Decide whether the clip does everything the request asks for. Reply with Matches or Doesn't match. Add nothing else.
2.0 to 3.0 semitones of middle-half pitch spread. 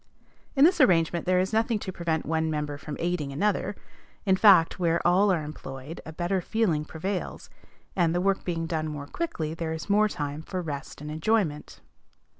Doesn't match